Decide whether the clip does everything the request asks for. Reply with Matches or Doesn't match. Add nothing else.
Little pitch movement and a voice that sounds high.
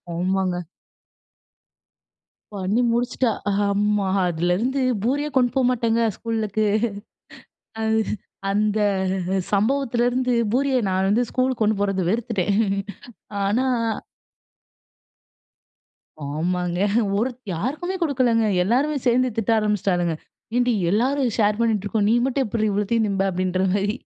Doesn't match